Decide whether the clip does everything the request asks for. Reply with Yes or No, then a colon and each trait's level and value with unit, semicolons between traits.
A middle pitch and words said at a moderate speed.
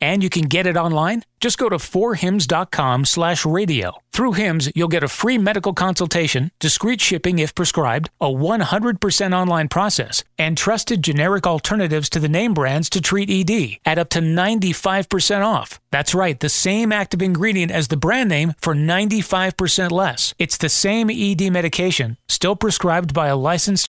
Yes: medium, 180 Hz; average, 165 wpm